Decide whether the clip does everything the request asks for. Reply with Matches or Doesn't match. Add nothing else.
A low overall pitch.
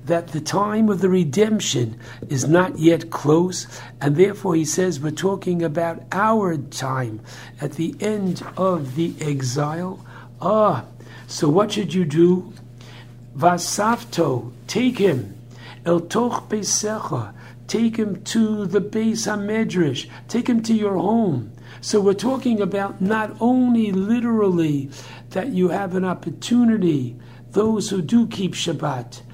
Doesn't match